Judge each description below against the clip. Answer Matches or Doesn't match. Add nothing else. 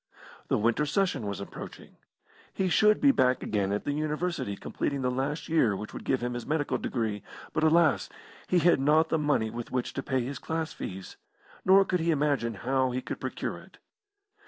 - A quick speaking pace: Doesn't match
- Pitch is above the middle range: Doesn't match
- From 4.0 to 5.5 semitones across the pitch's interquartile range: Matches